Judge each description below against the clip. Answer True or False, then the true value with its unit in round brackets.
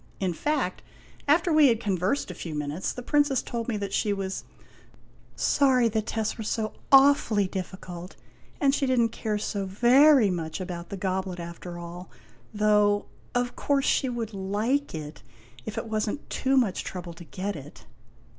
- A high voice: True (210 Hz)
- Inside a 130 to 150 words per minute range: False (175 wpm)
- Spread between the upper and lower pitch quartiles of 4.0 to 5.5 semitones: True (5.2 semitones)